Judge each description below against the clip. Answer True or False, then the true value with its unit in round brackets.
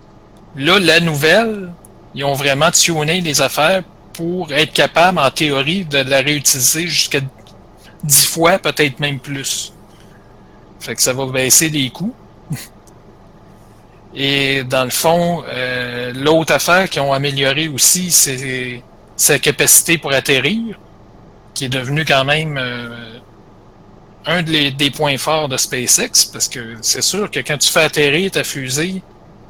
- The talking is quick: False (145 wpm)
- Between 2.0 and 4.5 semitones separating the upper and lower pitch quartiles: True (3.8 semitones)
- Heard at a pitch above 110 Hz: True (140 Hz)